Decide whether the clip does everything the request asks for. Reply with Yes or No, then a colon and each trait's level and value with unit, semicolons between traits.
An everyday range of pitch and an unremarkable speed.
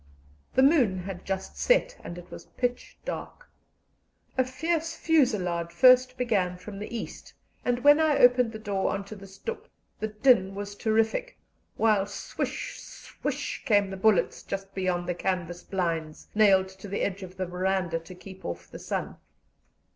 Yes: average, 5.0 semitones; average, 165 wpm